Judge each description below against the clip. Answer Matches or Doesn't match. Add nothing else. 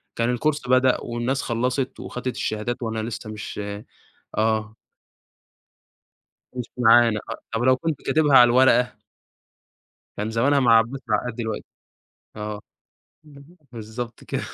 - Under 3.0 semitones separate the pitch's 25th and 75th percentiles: Matches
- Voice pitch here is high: Doesn't match